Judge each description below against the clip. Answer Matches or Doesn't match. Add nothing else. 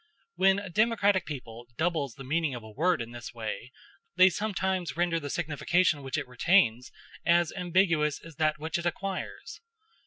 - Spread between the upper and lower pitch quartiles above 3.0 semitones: Matches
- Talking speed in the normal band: Matches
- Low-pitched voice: Doesn't match